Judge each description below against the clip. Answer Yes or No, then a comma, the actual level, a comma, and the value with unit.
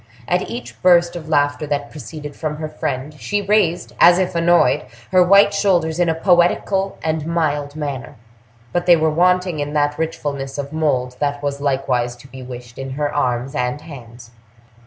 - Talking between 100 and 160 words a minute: No, average, 180 wpm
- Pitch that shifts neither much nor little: Yes, average, 3.8 semitones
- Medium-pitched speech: Yes, medium, 150 Hz